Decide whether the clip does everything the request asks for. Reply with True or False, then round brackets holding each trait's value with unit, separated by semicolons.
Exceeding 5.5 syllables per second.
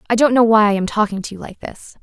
True (6.7 syllables/s)